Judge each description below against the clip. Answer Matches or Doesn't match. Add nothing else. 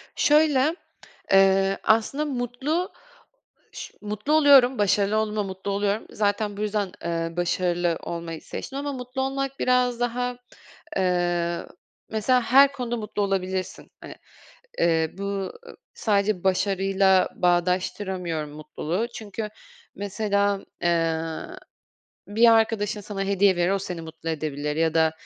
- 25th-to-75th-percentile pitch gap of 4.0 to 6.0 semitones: Matches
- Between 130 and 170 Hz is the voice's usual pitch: Doesn't match